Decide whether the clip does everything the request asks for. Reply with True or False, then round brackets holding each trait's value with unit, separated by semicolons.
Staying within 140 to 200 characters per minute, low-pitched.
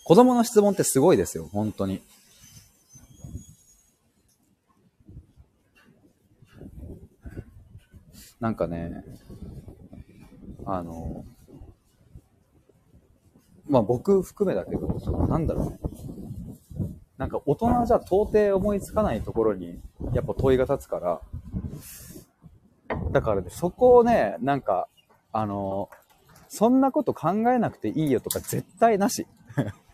True (195 characters per minute; 130 Hz)